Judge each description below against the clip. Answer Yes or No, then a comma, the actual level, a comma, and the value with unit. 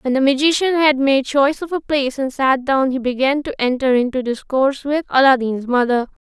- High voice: Yes, very high, 270 Hz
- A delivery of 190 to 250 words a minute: Yes, average, 200 wpm